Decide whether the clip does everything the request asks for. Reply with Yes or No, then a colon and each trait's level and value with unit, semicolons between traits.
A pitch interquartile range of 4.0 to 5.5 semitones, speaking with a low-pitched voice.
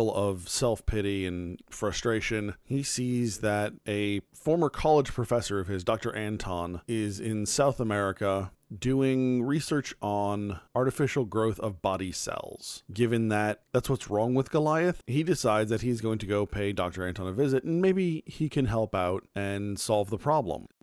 Yes: average, 4.6 semitones; low, 110 Hz